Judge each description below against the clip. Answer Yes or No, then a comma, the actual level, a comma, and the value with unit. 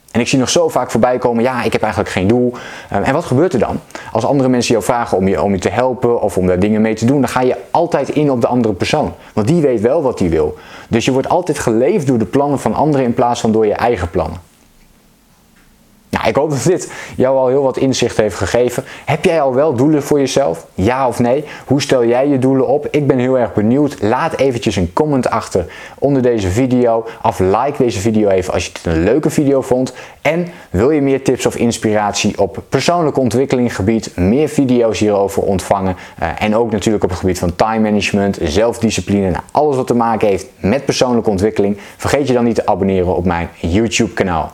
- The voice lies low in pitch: Yes, low, 115 Hz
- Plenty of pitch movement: No, average, 4.2 semitones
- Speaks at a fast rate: Yes, fast, 220 wpm